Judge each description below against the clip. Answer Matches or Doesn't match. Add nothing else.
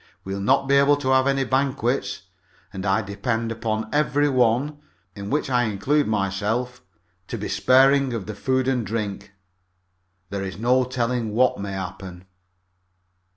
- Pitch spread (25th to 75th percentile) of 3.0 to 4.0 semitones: Doesn't match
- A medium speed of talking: Matches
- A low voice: Matches